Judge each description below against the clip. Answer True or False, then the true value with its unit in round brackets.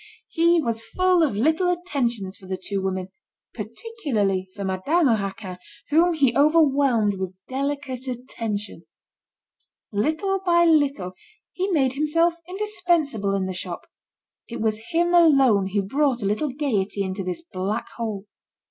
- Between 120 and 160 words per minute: True (140 wpm)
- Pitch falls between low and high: False (255 Hz)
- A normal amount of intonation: False (8.2 semitones)